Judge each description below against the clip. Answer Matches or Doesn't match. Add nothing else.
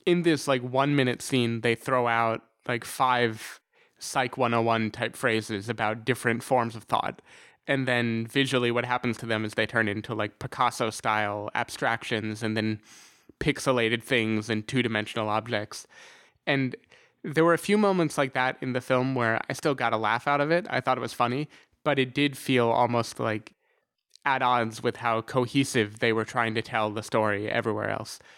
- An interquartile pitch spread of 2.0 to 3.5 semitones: Matches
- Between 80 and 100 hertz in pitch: Doesn't match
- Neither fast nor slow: Matches